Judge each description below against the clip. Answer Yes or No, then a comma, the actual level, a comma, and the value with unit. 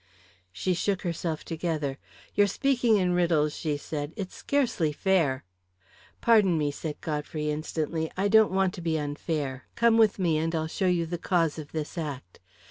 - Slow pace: No, average, 170 wpm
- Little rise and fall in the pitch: No, average, 3.9 semitones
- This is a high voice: No, medium, 165 Hz